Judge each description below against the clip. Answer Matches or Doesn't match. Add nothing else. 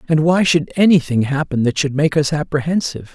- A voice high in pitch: Doesn't match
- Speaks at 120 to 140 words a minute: Doesn't match